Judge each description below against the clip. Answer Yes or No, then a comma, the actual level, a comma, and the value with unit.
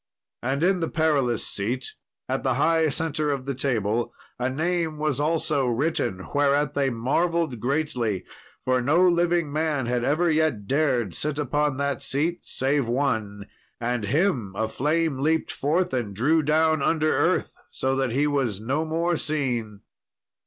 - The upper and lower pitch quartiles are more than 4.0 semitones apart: Yes, average, 4.4 semitones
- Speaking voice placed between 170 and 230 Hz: No, medium, 140 Hz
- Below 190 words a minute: Yes, average, 155 wpm